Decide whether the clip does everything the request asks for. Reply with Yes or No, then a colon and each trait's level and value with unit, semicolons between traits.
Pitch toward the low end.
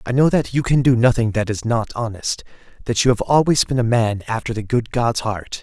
Yes: low, 120 Hz